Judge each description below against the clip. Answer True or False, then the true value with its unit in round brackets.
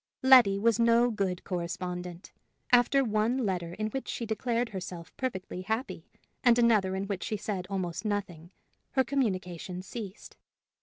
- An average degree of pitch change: True (4.2 semitones)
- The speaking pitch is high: True (205 Hz)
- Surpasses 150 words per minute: False (145 wpm)